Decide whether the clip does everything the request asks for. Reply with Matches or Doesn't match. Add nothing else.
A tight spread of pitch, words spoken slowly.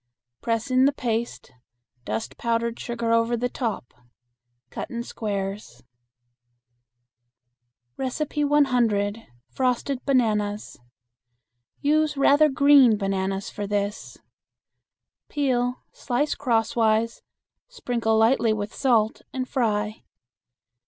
Doesn't match